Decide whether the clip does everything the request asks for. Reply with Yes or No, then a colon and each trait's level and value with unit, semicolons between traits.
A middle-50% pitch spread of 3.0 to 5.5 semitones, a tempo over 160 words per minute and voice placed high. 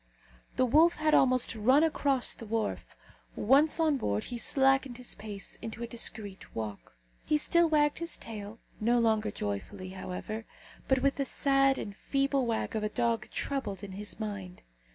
Yes: average, 4.7 semitones; average, 170 wpm; high, 235 Hz